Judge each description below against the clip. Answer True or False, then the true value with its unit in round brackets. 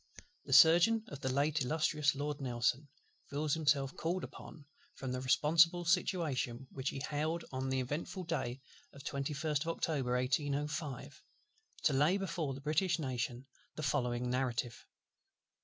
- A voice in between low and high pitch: True (145 Hz)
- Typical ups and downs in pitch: True (3.4 semitones)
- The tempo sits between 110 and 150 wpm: True (145 wpm)